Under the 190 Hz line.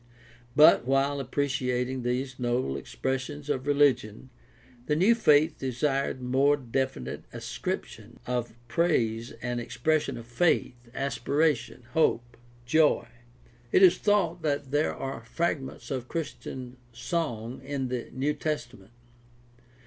Yes: low, 135 Hz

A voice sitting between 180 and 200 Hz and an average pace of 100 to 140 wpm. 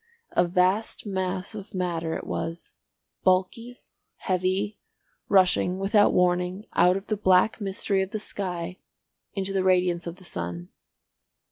Yes: medium, 185 Hz; slow, 135 wpm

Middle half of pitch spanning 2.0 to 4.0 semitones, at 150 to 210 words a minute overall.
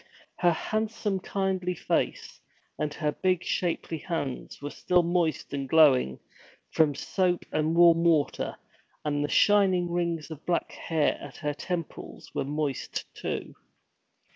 No: average, 3.3 semitones; slow, 135 wpm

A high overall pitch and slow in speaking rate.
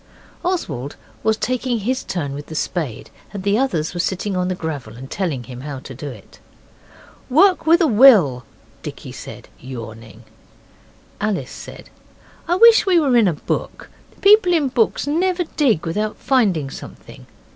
No: high, 195 Hz; average, 160 wpm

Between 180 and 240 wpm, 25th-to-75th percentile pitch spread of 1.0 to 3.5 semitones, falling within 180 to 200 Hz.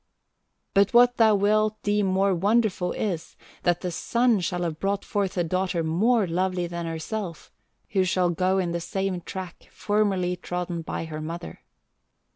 No: average, 160 wpm; average, 3.0 semitones; medium, 185 Hz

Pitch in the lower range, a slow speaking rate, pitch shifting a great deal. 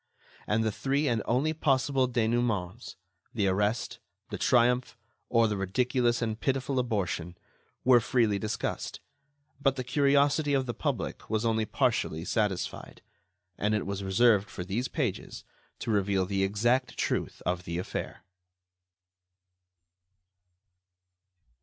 No: low, 115 Hz; slow, 120 wpm; average, 4.3 semitones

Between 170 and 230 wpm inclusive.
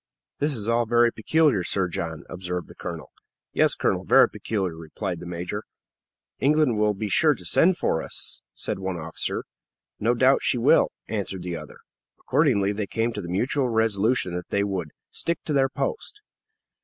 Yes: average, 175 wpm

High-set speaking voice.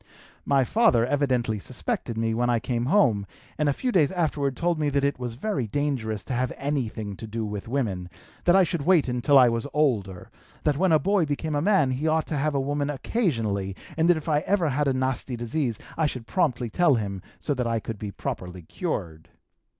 No: low, 135 Hz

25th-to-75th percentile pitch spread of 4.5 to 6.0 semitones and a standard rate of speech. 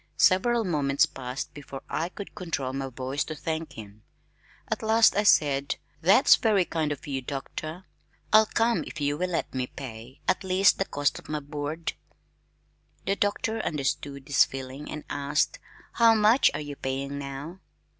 Yes: wide, 5.5 semitones; average, 165 wpm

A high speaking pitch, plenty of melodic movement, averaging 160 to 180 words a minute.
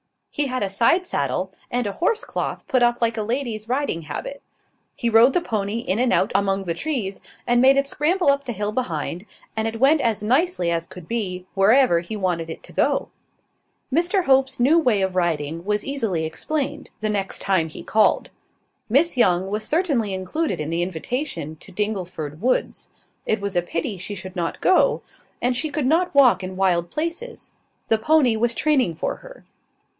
No: high, 220 Hz; wide, 6.8 semitones; average, 190 wpm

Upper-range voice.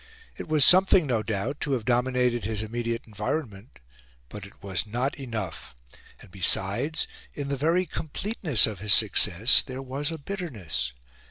No: low, 120 Hz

